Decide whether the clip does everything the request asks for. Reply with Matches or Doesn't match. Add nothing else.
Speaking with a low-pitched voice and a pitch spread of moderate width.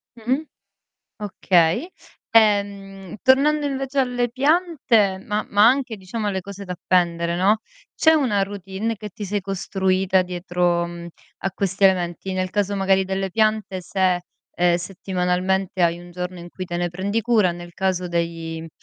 Doesn't match